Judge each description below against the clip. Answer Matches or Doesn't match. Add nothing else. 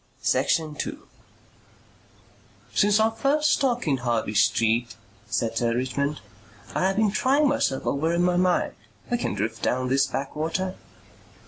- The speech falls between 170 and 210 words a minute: Doesn't match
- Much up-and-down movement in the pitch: Matches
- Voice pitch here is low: Doesn't match